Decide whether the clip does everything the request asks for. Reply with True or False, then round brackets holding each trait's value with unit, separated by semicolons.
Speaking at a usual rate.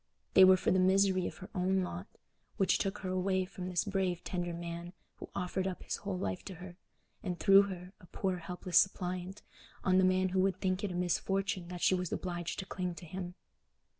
False (215 wpm)